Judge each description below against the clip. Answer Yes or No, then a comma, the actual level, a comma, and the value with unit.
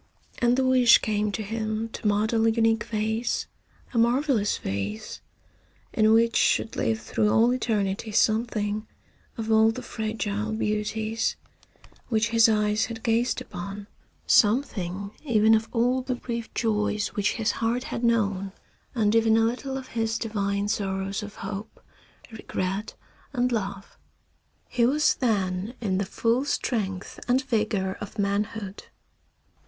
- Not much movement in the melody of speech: Yes, narrow, 2.2 semitones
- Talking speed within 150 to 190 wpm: No, average, 140 wpm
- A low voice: No, high, 220 Hz